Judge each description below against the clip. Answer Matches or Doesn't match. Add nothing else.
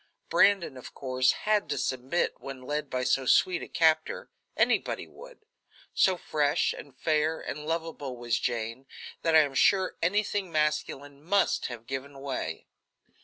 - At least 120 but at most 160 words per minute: Matches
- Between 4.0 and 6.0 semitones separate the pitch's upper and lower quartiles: Matches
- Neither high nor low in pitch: Matches